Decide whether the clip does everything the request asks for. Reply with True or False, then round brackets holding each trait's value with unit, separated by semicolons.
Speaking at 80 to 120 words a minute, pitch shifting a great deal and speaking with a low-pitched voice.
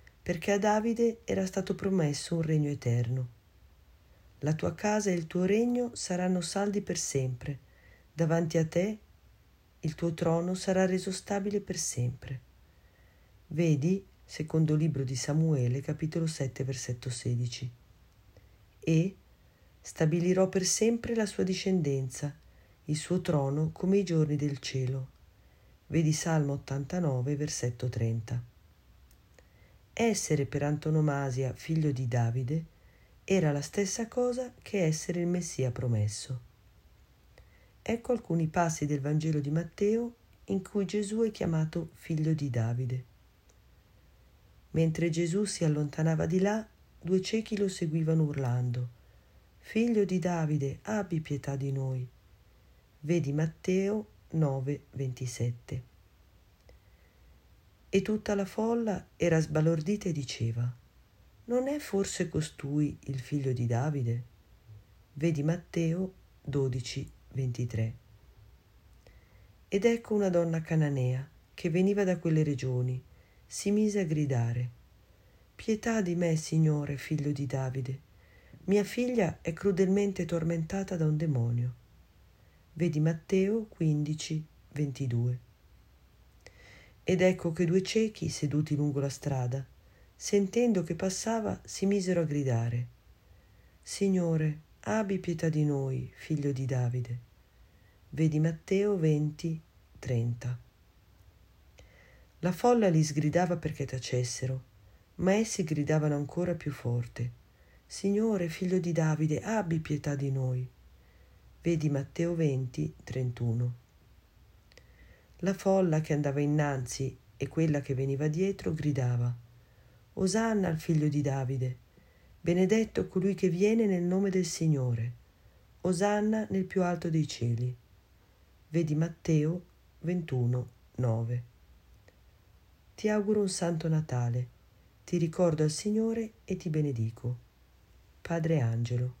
False (115 wpm; 6.5 semitones; 150 Hz)